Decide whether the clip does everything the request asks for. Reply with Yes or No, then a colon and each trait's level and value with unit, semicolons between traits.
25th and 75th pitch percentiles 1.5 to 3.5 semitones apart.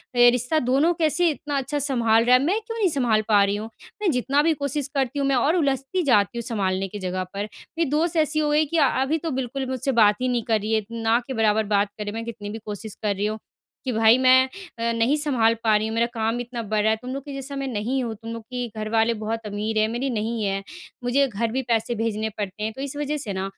No: average, 4.0 semitones